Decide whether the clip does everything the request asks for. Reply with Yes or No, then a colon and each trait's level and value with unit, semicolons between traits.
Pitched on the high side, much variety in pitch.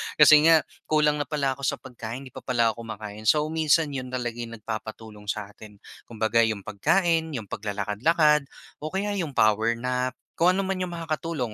No: low, 125 Hz; wide, 6.0 semitones